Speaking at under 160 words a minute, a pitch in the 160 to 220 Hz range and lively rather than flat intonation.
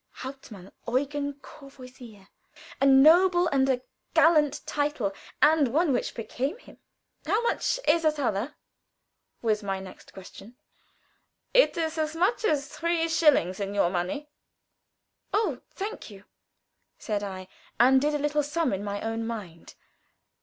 No: average, 140 wpm; very high, 275 Hz; wide, 6.7 semitones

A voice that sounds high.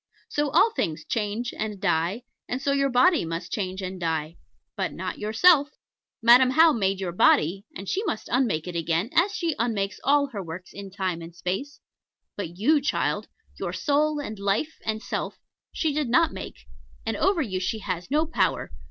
Yes: high, 215 Hz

